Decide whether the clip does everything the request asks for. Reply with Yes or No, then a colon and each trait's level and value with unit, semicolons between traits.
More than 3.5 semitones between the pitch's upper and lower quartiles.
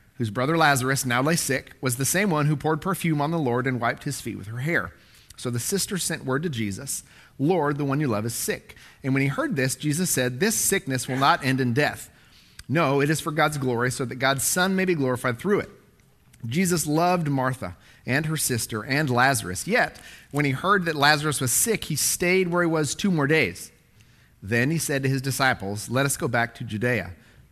Yes: average, 4.1 semitones